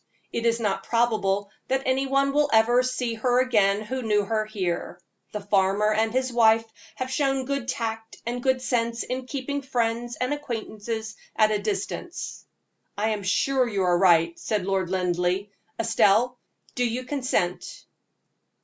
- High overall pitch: Yes, high, 230 Hz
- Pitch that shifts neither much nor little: Yes, average, 3.8 semitones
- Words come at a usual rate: Yes, average, 160 wpm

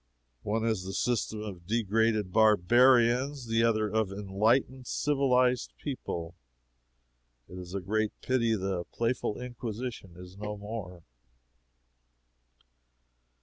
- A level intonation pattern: No, average, 3.7 semitones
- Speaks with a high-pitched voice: No, low, 110 Hz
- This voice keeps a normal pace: No, slow, 105 wpm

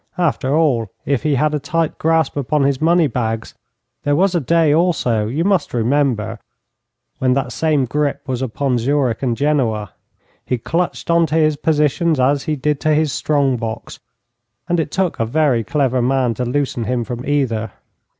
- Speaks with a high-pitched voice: No, medium, 140 Hz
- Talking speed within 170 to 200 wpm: Yes, average, 180 wpm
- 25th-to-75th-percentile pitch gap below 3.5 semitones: No, average, 4.0 semitones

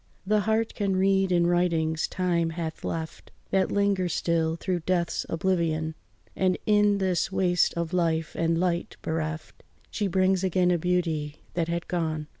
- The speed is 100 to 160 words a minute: Yes, average, 155 wpm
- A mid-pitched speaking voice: Yes, medium, 175 Hz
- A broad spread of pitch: No, narrow, 2.4 semitones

